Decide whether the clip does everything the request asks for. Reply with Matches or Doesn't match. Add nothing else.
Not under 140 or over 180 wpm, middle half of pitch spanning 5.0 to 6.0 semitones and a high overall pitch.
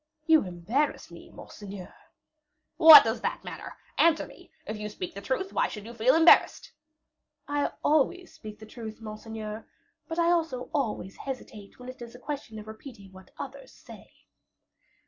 Matches